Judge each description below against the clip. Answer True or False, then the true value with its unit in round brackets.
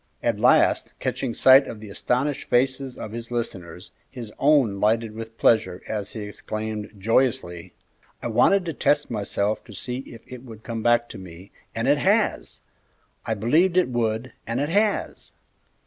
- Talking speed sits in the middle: True (165 wpm)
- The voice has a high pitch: False (115 Hz)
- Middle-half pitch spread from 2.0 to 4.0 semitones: True (3.5 semitones)